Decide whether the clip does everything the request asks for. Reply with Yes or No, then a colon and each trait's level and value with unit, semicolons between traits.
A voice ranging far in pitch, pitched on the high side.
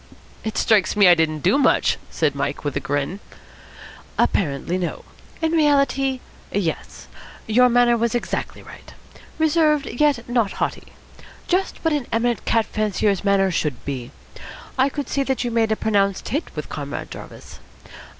Yes: wide, 6.5 semitones; high, 225 Hz